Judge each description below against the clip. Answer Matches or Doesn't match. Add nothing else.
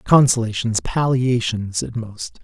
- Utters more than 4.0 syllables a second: Doesn't match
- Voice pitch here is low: Matches